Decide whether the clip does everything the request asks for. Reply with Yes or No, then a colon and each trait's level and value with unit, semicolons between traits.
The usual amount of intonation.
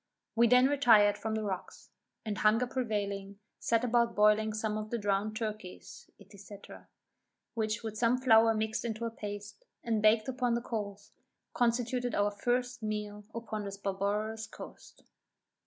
No: narrow, 2.2 semitones